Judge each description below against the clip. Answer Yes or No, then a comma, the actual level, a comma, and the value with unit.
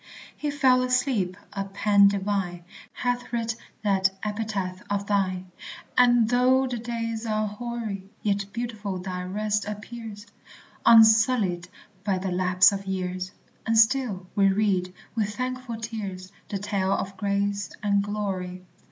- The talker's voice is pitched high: Yes, high, 205 Hz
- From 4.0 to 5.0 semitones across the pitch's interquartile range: No, average, 3.0 semitones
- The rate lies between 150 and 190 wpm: No, slow, 135 wpm